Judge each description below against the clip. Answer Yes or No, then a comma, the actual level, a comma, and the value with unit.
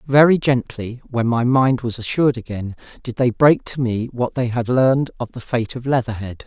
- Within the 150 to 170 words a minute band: No, fast, 205 wpm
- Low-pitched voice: Yes, low, 120 Hz